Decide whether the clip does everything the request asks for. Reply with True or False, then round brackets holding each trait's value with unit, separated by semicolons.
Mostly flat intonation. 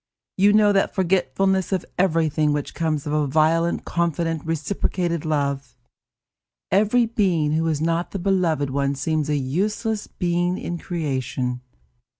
False (4.1 semitones)